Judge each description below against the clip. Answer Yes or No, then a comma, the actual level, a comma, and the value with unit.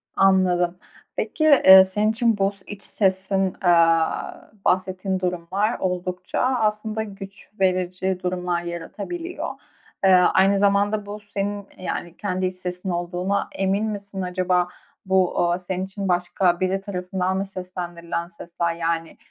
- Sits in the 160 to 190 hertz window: Yes, medium, 185 Hz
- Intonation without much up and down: Yes, narrow, 1.9 semitones